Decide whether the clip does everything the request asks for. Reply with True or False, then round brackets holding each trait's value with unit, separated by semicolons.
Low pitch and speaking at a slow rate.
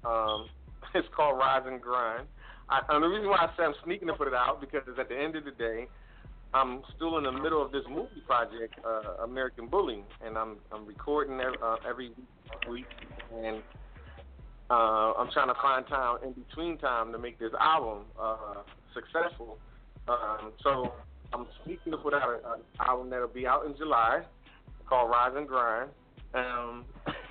False (125 Hz; 180 wpm)